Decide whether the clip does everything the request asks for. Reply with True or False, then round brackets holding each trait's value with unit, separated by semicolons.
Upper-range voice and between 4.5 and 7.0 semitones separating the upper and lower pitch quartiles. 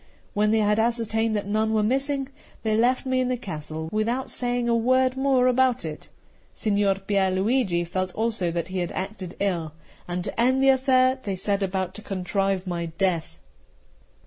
True (210 Hz; 5.0 semitones)